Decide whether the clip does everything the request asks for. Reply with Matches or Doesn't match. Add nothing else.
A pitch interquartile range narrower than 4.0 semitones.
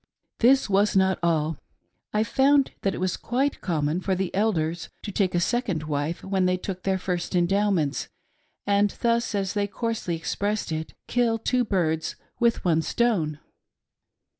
Doesn't match